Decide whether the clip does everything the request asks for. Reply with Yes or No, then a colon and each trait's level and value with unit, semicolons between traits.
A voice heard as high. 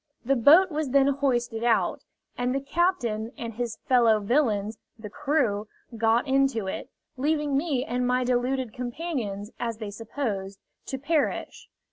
Yes: high, 245 Hz